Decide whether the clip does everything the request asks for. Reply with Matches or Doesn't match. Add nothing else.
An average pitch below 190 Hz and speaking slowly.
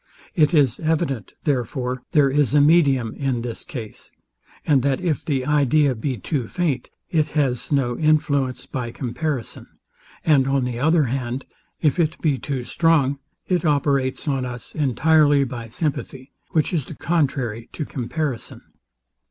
Doesn't match